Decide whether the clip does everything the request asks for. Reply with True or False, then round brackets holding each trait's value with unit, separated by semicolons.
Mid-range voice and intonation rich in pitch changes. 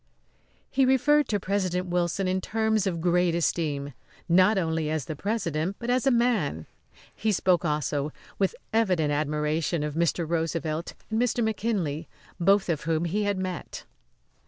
False (180 Hz; 4.7 semitones)